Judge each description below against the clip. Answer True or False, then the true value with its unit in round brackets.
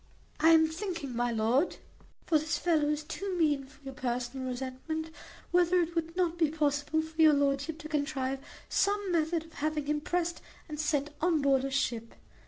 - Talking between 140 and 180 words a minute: False (190 wpm)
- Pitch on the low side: False (305 Hz)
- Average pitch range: True (3.1 semitones)